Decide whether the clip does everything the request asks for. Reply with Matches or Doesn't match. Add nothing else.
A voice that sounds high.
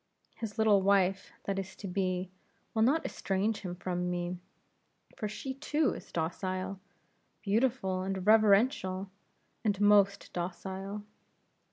Matches